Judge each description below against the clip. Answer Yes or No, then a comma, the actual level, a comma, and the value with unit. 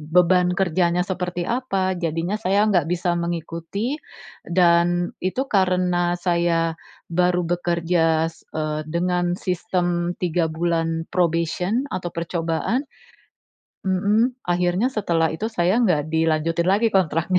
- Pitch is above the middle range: No, medium, 175 Hz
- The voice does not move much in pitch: Yes, narrow, 1.9 semitones